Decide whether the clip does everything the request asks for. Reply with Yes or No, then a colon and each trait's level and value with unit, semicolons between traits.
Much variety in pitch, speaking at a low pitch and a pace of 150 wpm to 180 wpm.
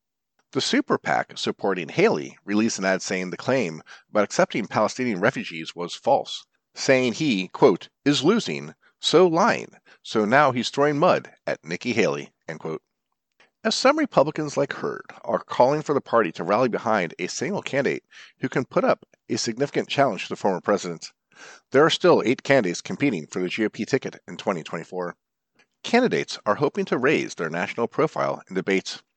Yes: wide, 7.3 semitones; low, 110 Hz; average, 170 wpm